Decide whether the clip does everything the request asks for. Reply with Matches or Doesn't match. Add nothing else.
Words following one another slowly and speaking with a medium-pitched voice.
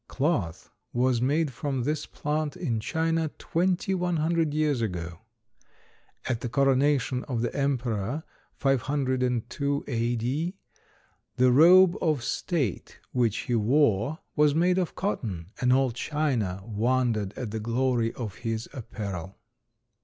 Doesn't match